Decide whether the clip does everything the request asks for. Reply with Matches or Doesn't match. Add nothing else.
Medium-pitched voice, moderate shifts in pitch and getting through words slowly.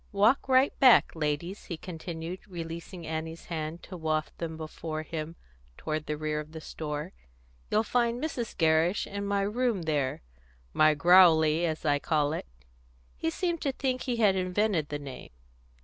Doesn't match